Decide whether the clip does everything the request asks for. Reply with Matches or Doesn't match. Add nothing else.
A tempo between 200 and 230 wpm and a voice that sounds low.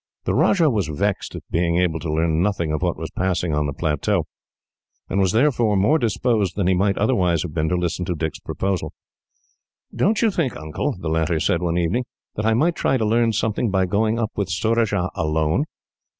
Matches